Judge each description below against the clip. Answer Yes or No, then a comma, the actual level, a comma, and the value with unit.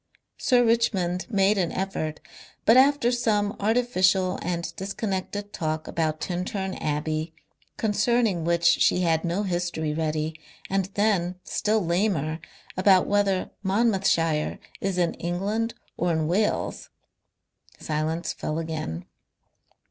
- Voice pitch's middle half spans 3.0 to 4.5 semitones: Yes, average, 4.0 semitones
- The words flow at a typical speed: No, slow, 110 wpm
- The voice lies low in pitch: No, medium, 185 Hz